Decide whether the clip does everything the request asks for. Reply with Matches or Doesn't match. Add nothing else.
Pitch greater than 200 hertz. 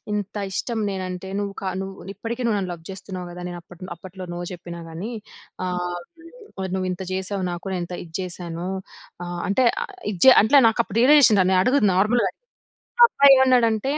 Doesn't match